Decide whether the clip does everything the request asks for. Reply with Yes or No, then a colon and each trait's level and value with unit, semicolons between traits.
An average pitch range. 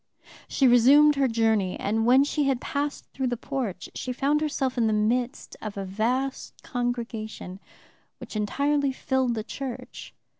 Yes: average, 3.6 semitones